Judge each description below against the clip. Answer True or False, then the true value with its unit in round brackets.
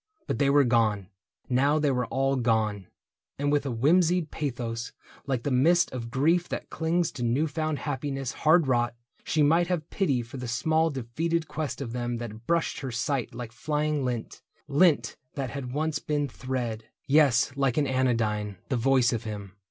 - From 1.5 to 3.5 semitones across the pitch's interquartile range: False (4.1 semitones)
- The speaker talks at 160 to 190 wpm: True (185 wpm)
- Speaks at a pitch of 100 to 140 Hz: True (135 Hz)